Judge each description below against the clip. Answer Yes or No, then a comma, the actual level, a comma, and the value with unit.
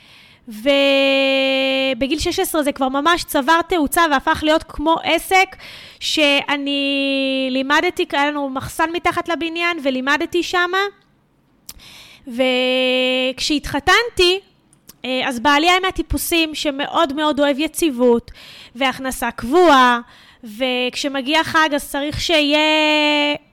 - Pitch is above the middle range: Yes, very high, 290 Hz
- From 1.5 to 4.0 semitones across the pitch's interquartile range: Yes, average, 3.6 semitones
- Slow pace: Yes, slow, 90 wpm